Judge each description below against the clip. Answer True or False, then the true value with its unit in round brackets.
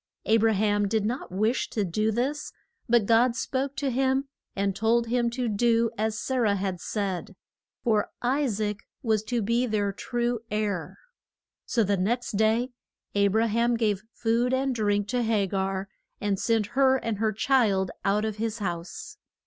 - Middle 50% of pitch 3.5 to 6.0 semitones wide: False (2.9 semitones)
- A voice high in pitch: True (220 Hz)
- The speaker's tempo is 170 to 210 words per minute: True (175 wpm)